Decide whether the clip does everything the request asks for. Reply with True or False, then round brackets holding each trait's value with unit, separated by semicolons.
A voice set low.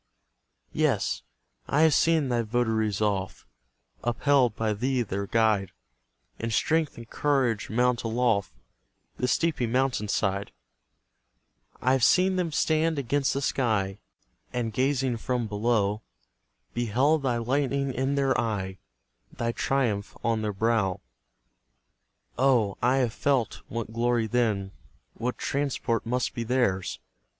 True (120 Hz)